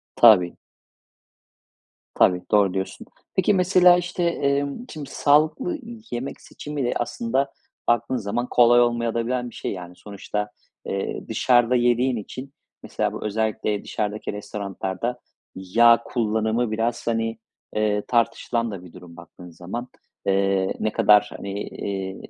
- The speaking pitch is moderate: No, low, 115 Hz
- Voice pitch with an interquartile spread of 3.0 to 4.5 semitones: Yes, average, 3.6 semitones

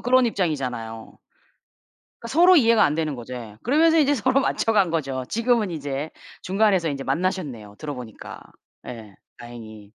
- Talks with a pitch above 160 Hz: No, medium, 155 Hz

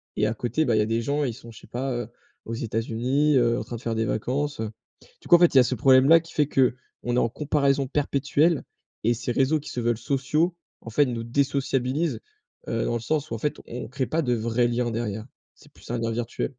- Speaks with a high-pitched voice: No, low, 125 Hz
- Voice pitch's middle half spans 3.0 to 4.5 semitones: Yes, average, 3.5 semitones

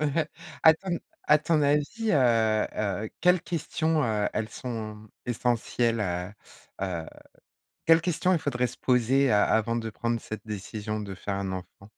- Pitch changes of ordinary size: No, wide, 5.9 semitones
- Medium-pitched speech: No, low, 115 Hz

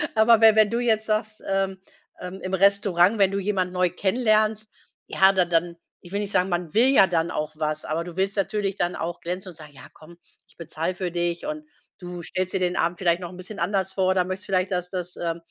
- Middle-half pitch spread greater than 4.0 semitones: No, narrow, 2.6 semitones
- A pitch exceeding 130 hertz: Yes, medium, 185 Hz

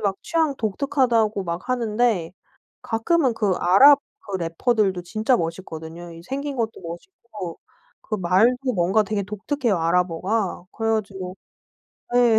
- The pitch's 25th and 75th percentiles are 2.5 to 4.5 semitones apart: No, average, 5.2 semitones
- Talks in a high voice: Yes, high, 215 Hz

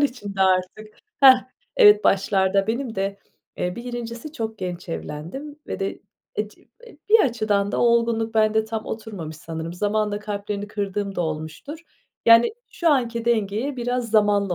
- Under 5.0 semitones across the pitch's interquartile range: Yes, average, 3.1 semitones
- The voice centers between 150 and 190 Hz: No, high, 215 Hz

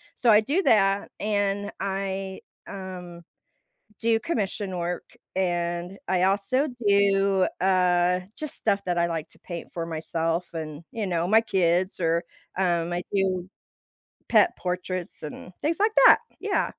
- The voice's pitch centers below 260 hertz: Yes, high, 190 Hz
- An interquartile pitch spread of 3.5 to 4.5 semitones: No, narrow, 2.5 semitones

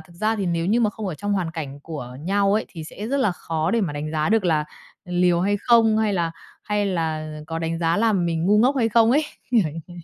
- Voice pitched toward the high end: No, medium, 180 Hz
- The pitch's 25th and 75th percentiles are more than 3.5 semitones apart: Yes, average, 4.7 semitones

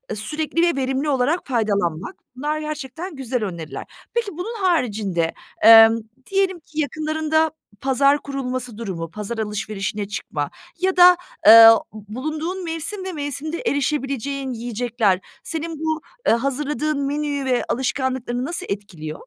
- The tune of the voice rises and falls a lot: Yes, wide, 5.8 semitones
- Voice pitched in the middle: No, very high, 270 Hz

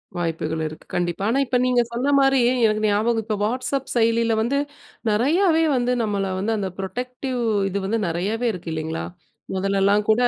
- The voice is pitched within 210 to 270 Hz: Yes, high, 225 Hz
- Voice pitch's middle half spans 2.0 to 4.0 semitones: No, average, 4.4 semitones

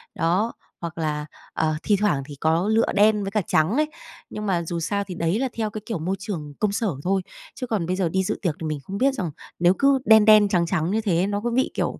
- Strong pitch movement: No, average, 4.3 semitones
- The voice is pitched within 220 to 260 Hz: No, high, 195 Hz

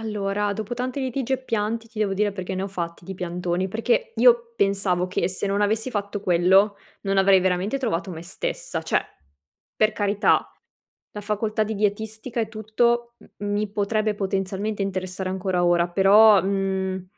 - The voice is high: Yes, high, 200 Hz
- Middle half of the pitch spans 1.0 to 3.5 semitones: Yes, narrow, 2.5 semitones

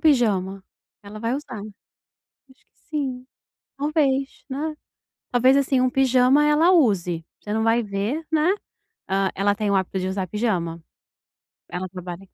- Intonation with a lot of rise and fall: Yes, wide, 5.9 semitones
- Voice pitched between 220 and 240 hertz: Yes, high, 230 Hz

